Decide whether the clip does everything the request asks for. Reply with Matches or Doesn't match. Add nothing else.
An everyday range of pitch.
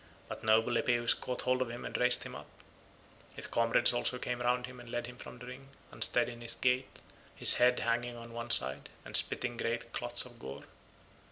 Doesn't match